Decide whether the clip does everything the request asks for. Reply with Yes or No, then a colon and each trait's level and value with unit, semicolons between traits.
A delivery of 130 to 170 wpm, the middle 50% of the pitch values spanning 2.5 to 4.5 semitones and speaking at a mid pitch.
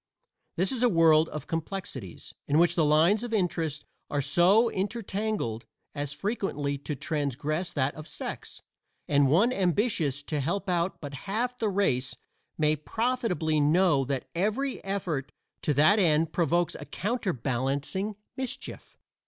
No: slow, 135 wpm; wide, 5.6 semitones; medium, 165 Hz